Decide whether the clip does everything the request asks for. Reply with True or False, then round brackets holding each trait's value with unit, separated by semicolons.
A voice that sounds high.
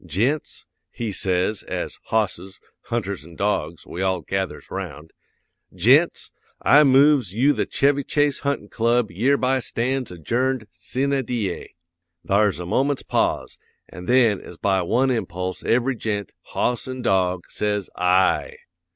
False (110 Hz)